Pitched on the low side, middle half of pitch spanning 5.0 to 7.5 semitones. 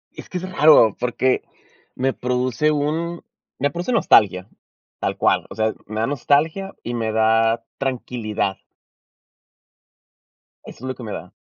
Yes: low, 125 Hz; average, 5.3 semitones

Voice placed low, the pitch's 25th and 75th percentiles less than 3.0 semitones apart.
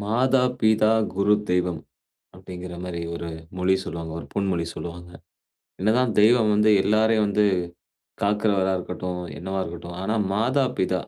No: very low, 95 Hz; average, 3.3 semitones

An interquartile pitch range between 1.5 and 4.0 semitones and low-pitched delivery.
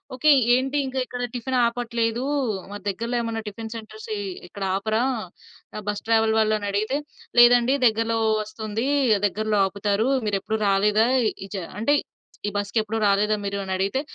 No: narrow, 2.4 semitones; high, 220 Hz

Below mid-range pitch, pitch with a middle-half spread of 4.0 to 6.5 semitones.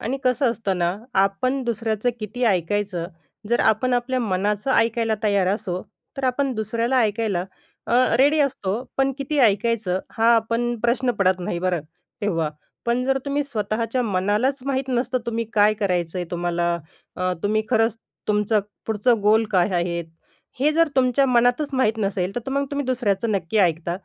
No: high, 220 Hz; average, 4.4 semitones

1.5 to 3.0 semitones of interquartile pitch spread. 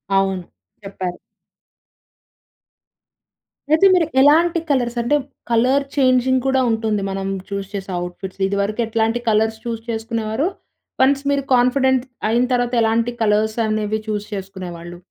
No: average, 4.2 semitones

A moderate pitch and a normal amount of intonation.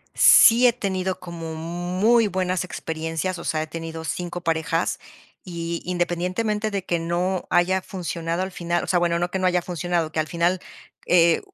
No: medium, 175 Hz; narrow, 1.8 semitones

